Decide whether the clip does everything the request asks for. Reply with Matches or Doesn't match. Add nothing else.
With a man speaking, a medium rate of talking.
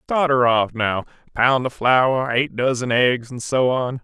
Matches